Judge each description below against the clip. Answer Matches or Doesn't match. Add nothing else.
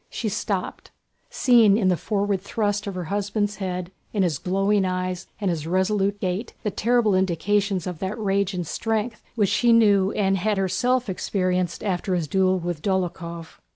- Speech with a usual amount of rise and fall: Doesn't match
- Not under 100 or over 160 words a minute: Doesn't match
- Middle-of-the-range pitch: Doesn't match